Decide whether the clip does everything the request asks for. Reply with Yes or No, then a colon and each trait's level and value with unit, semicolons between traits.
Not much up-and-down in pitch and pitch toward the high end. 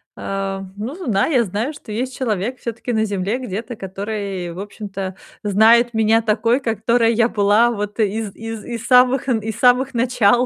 No: average, 3.0 semitones; high, 225 Hz